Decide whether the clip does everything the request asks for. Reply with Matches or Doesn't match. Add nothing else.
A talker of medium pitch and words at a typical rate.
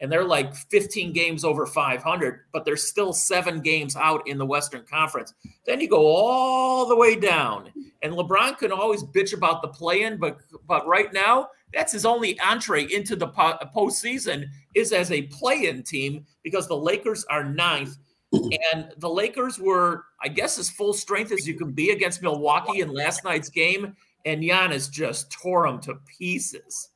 Matches